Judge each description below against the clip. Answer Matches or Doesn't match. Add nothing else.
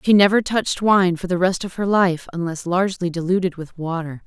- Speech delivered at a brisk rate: Matches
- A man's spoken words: Doesn't match